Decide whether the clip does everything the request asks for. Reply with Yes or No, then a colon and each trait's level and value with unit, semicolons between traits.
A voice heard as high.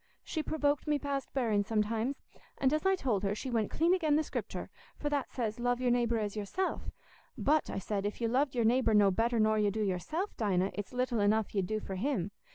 Yes: high, 230 Hz